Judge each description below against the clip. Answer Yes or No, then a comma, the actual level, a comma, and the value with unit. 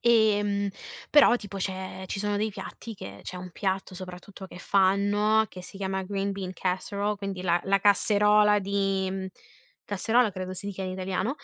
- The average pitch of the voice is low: No, high, 195 Hz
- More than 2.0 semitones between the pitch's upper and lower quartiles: No, narrow, 1.7 semitones